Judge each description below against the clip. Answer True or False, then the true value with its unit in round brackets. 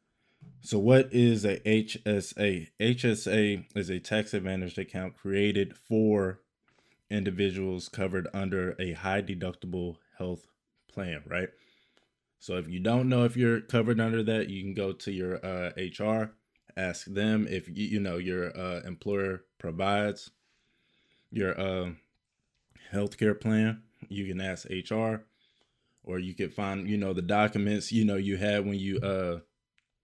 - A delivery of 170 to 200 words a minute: False (145 wpm)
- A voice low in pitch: True (100 Hz)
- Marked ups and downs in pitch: False (2.6 semitones)